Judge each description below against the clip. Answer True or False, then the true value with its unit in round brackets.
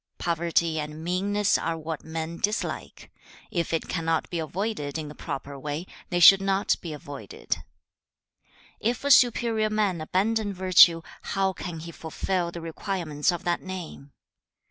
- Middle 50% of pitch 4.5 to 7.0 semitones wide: False (3.4 semitones)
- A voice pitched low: False (170 Hz)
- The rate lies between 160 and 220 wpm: False (150 wpm)